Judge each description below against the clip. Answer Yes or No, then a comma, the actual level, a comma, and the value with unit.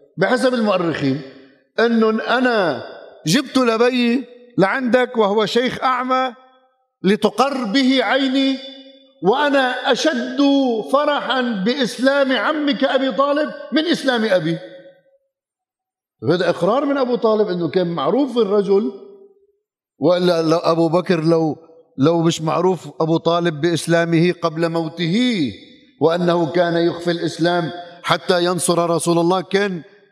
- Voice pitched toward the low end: No, high, 220 Hz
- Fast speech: No, average, 105 wpm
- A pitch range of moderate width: No, wide, 7.5 semitones